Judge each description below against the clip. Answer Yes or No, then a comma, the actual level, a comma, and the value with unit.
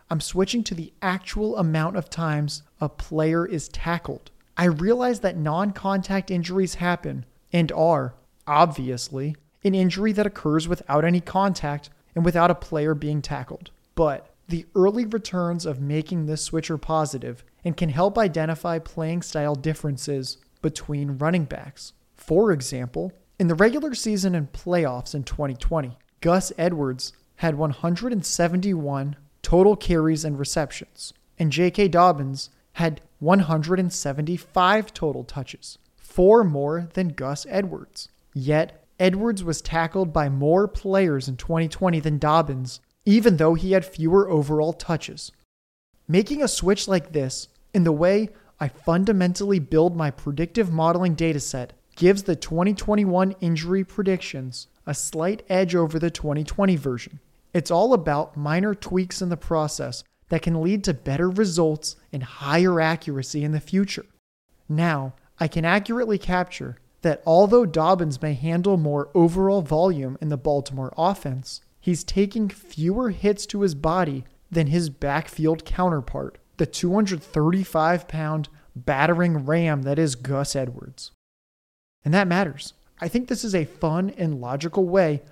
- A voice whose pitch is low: No, medium, 165 Hz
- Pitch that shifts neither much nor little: Yes, average, 3.9 semitones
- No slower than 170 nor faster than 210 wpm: No, average, 140 wpm